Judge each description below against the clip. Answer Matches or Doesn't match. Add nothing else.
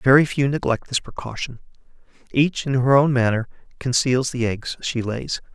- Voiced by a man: Matches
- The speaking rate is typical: Matches